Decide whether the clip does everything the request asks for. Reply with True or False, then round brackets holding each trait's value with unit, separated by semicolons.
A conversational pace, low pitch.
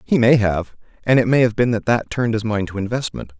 False (265 wpm; 110 Hz)